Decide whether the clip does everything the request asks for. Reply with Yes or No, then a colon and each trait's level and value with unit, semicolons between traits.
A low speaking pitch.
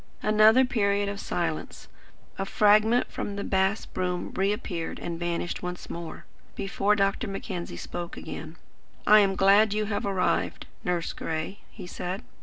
No: high, 195 Hz